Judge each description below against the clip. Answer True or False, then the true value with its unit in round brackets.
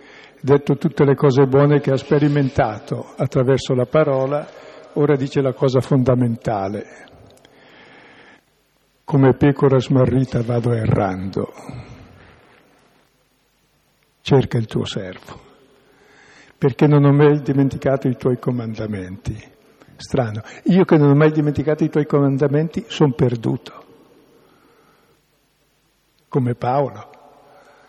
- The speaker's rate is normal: False (100 wpm)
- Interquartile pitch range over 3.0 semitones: False (2.4 semitones)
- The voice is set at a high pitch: False (140 Hz)